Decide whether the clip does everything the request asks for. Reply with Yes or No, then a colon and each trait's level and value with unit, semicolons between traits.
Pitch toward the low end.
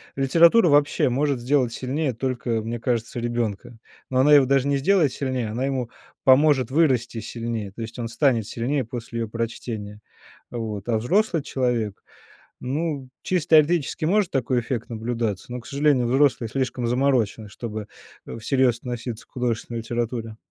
Yes: low, 125 Hz